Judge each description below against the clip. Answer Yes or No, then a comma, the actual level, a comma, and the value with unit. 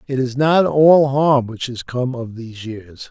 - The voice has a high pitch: No, low, 130 Hz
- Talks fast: Yes, fast, 210 wpm